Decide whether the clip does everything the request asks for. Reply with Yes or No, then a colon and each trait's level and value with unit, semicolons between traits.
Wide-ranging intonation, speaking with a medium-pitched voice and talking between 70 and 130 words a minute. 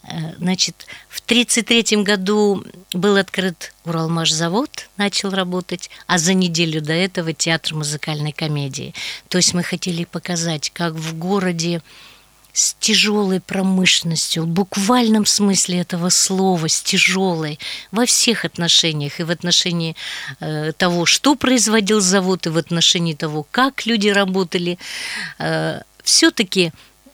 No: average, 3.4 semitones; medium, 180 Hz; average, 115 wpm